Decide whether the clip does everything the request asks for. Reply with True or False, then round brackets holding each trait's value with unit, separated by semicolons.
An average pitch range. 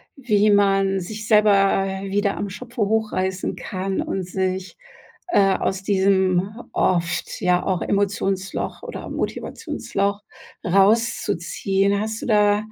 False (1.5 semitones)